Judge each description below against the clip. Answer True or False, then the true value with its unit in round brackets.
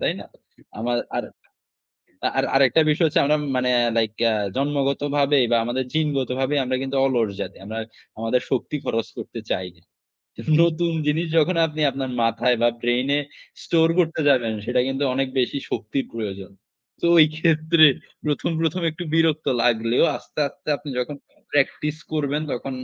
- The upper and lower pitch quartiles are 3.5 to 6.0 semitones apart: True (3.9 semitones)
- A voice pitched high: False (135 Hz)